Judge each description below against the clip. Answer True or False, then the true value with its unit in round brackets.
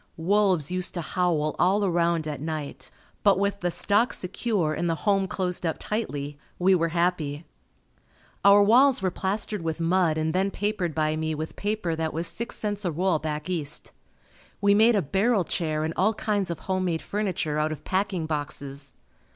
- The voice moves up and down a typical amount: True (4.2 semitones)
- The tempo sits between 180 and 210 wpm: True (185 wpm)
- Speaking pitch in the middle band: True (180 Hz)